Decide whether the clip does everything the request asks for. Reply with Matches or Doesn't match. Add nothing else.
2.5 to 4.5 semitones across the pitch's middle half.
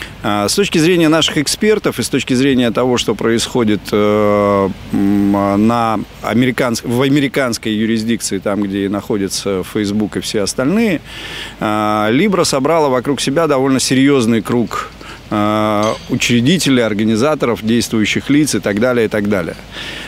Matches